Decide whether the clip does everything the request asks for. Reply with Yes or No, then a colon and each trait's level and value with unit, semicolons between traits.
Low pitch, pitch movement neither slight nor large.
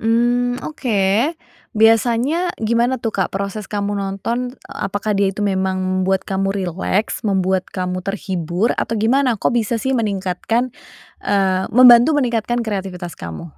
No: high, 205 Hz; average, 3.8 semitones